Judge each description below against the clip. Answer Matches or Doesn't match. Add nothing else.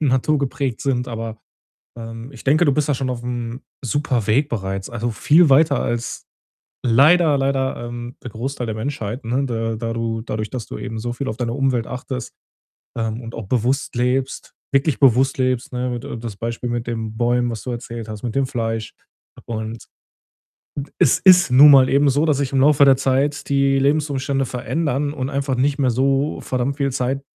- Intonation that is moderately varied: Matches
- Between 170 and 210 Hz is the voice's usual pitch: Doesn't match